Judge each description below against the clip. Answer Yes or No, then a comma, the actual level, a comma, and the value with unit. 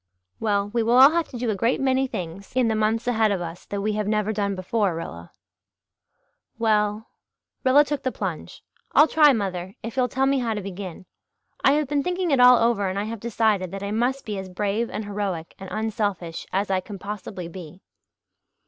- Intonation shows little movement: No, average, 3.9 semitones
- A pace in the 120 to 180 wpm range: No, fast, 205 wpm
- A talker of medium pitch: No, high, 215 Hz